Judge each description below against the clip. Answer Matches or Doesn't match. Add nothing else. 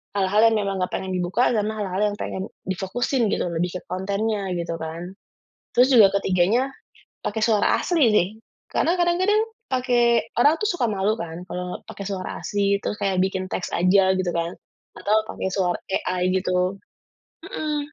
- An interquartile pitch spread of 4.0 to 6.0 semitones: Matches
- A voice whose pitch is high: Matches